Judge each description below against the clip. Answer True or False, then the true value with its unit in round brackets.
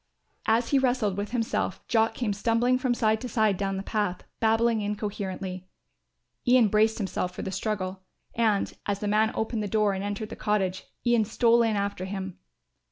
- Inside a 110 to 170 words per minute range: False (180 wpm)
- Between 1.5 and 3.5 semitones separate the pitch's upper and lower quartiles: True (2.4 semitones)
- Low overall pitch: False (215 Hz)